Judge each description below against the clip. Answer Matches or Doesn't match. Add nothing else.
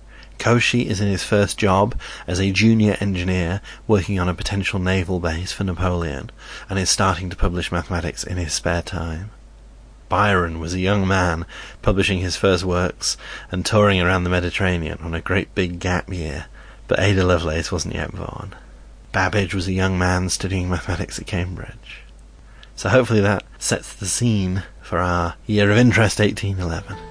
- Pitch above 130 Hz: Doesn't match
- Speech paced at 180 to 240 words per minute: Doesn't match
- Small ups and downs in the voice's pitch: Matches